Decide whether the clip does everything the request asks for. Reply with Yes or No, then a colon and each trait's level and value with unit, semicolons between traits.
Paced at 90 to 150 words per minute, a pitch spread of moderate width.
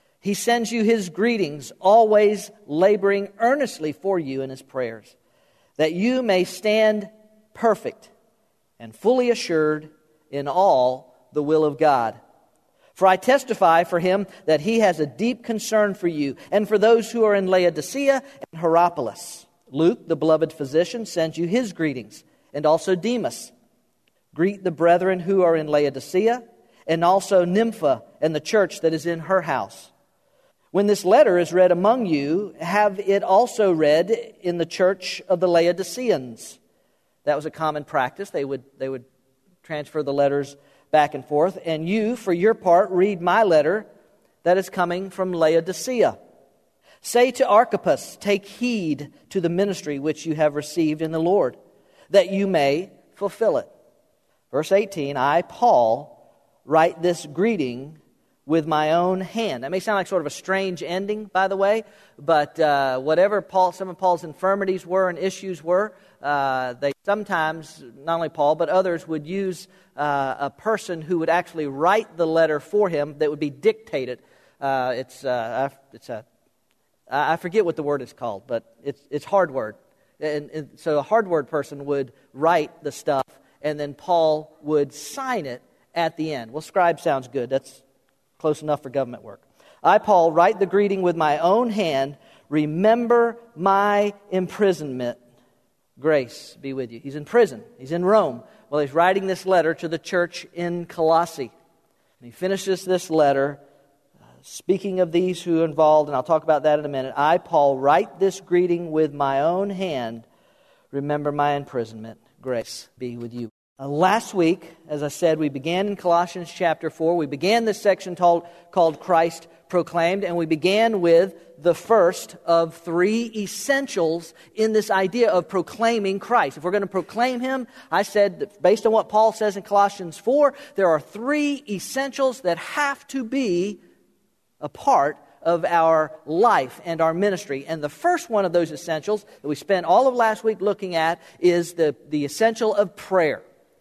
No: average, 170 wpm; average, 4.9 semitones